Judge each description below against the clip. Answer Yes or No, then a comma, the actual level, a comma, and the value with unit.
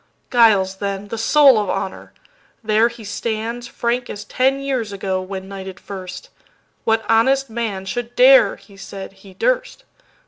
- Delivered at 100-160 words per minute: Yes, slow, 135 wpm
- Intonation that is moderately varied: Yes, average, 3.8 semitones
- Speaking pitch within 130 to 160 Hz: No, high, 220 Hz